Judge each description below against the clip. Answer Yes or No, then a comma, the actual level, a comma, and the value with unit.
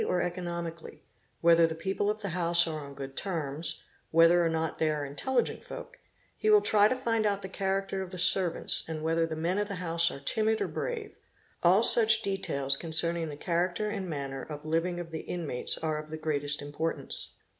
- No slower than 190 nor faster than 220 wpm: Yes, fast, 205 wpm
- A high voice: No, medium, 170 Hz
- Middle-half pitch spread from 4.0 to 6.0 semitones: No, average, 3.5 semitones